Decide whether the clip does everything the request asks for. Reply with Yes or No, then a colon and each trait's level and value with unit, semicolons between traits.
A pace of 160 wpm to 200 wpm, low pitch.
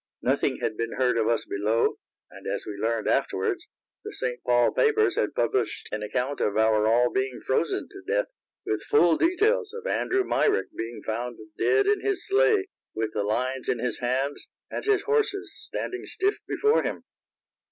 Yes: average, 175 wpm; low, 130 Hz